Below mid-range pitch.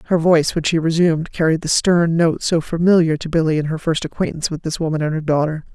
No: medium, 160 Hz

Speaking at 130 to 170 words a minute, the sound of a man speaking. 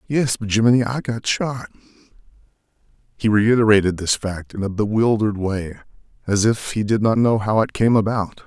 Yes: average, 165 wpm; male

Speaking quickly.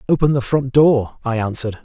No: average, 195 wpm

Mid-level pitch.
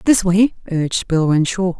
Yes: medium, 180 Hz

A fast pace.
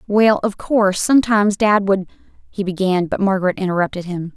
No: average, 150 wpm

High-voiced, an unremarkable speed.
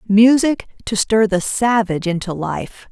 Yes: high, 210 Hz; average, 145 wpm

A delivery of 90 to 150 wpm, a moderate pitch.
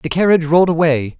No: average, 200 wpm; medium, 160 Hz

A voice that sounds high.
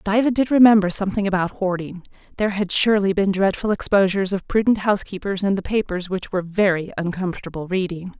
Yes: high, 195 Hz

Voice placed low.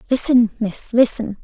No: high, 230 Hz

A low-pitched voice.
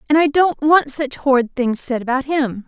No: very high, 275 Hz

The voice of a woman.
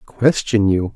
No: male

